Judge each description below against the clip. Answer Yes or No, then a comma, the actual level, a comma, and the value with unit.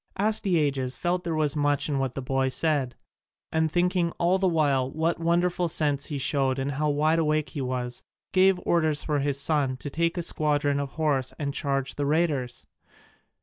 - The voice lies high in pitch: No, medium, 150 Hz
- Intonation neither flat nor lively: Yes, average, 3.3 semitones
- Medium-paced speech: Yes, average, 185 wpm